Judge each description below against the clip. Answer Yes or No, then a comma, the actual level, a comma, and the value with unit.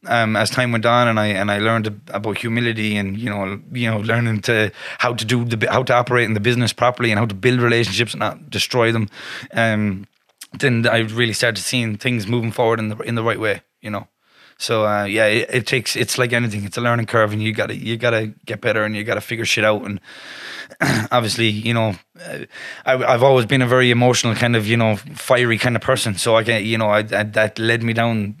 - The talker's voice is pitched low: Yes, low, 115 Hz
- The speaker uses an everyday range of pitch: No, narrow, 2.0 semitones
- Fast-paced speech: Yes, fast, 245 wpm